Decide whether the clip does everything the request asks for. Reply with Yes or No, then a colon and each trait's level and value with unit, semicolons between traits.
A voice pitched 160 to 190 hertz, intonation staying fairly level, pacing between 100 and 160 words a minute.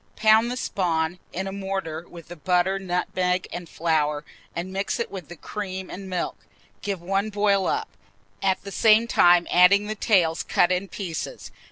No: medium, 185 Hz; narrow, 2.2 semitones; average, 175 wpm